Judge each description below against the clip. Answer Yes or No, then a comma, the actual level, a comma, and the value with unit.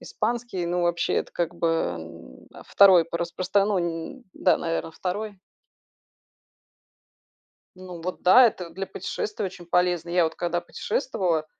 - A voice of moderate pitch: Yes, medium, 175 Hz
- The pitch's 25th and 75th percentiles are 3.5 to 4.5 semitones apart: No, narrow, 2.4 semitones